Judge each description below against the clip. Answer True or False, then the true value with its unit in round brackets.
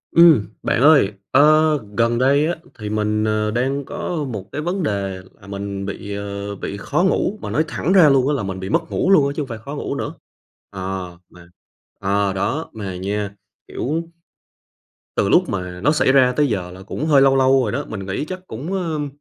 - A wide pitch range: True (6.9 semitones)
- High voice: False (120 Hz)